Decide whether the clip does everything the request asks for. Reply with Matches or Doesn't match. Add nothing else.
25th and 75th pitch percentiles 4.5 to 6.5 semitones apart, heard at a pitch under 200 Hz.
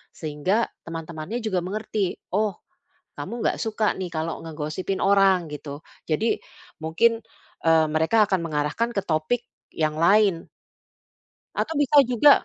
Matches